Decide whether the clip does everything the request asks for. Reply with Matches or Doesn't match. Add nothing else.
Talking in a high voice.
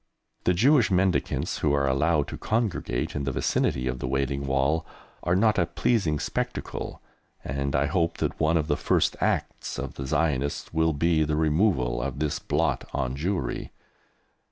Doesn't match